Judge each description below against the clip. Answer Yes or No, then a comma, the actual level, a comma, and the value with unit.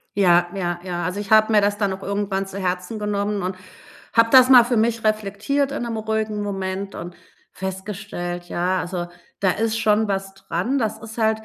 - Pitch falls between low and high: No, high, 200 Hz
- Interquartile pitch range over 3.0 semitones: No, narrow, 2.6 semitones